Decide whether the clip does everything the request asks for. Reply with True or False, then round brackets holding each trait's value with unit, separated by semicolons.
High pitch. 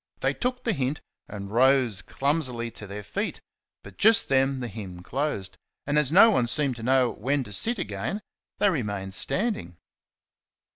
False (130 Hz)